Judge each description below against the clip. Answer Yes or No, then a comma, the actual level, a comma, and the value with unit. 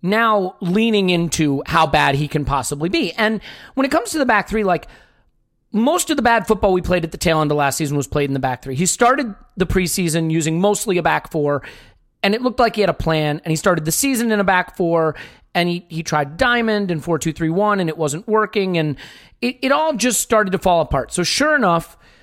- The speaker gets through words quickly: Yes, fast, 245 wpm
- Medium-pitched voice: Yes, medium, 180 Hz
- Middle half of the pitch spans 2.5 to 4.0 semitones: No, average, 5.3 semitones